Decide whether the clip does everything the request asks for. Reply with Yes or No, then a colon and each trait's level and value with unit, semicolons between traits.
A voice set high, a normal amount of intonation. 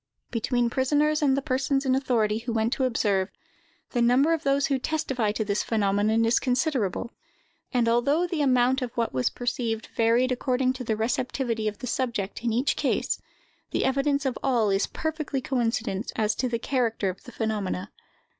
Yes: high, 245 Hz; average, 3.3 semitones